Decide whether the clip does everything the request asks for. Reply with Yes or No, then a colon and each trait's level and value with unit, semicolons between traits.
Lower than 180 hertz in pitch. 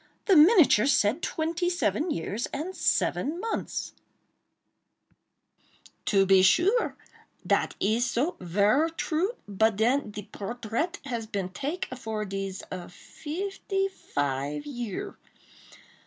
No: high, 240 Hz